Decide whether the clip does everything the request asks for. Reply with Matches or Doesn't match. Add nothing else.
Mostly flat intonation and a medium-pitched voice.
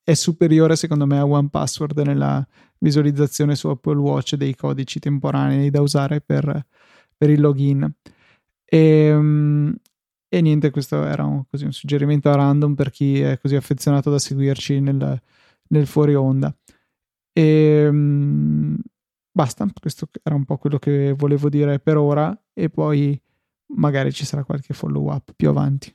Matches